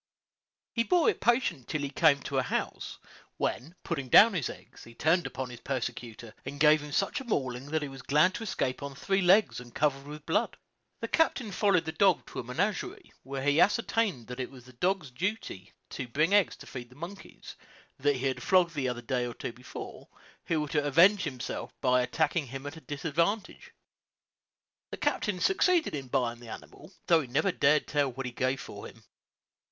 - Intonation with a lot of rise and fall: Yes, wide, 6.1 semitones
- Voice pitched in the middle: Yes, medium, 145 Hz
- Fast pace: Yes, fast, 210 wpm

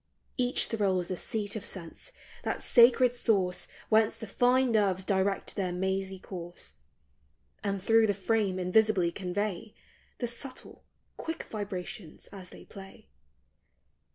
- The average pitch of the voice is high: Yes, high, 200 Hz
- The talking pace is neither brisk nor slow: No, slow, 125 wpm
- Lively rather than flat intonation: No, average, 3.2 semitones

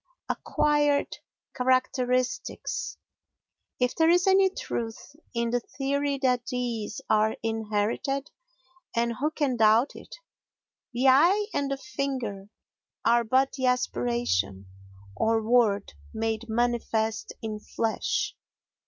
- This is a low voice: No, high, 245 Hz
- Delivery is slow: Yes, slow, 100 wpm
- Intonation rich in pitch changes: No, average, 4.0 semitones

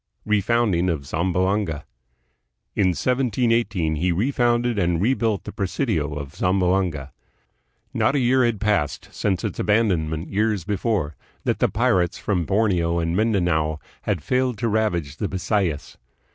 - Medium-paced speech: No, slow, 130 wpm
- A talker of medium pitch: No, very low, 95 Hz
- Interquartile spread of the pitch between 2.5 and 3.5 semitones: No, average, 5.0 semitones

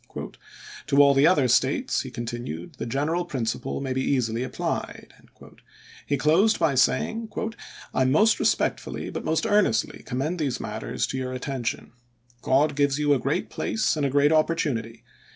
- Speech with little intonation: No, average, 3.5 semitones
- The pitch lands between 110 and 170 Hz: Yes, medium, 140 Hz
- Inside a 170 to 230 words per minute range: No, average, 160 wpm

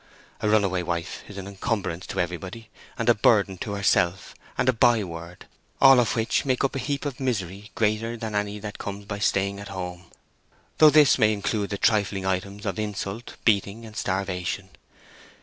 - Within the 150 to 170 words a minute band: Yes, average, 165 wpm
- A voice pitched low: Yes, low, 100 Hz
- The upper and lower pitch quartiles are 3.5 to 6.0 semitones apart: No, average, 2.9 semitones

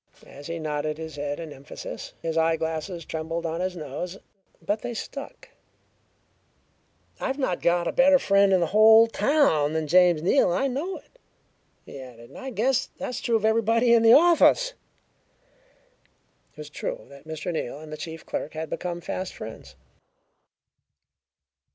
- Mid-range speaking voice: Yes, medium, 170 Hz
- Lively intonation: Yes, wide, 6.6 semitones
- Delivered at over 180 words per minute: No, average, 165 wpm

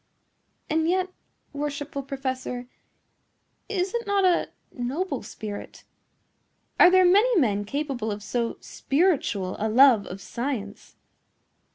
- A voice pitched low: No, very high, 275 Hz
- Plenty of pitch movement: Yes, wide, 8.0 semitones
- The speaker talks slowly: Yes, slow, 110 wpm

